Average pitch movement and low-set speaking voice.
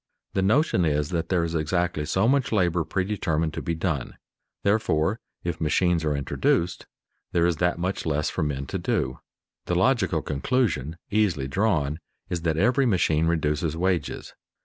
Yes: average, 3.6 semitones; very low, 85 Hz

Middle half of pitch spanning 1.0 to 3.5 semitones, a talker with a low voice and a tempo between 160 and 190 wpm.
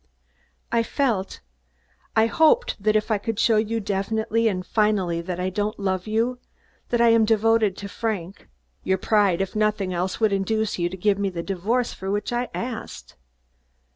No: average, 2.9 semitones; high, 210 Hz; average, 175 wpm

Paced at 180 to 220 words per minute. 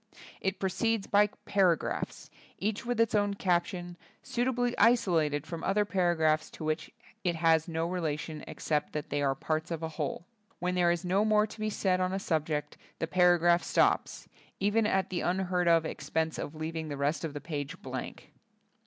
Yes: average, 190 wpm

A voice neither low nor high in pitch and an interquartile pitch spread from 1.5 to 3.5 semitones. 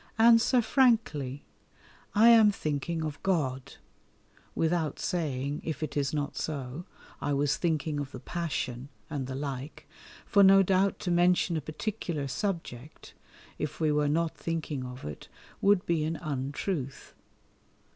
No: medium, 155 Hz; average, 4.2 semitones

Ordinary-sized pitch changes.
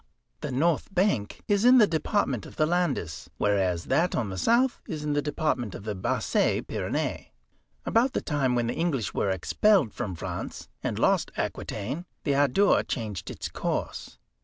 No: wide, 8.8 semitones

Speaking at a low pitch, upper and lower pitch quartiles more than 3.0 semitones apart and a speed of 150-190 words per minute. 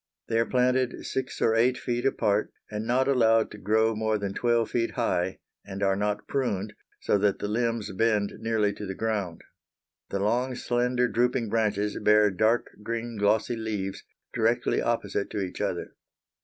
No: low, 110 Hz; narrow, 2.6 semitones; average, 170 wpm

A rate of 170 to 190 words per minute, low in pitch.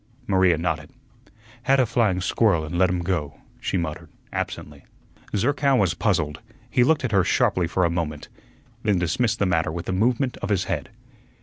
Yes: average, 180 wpm; very low, 95 Hz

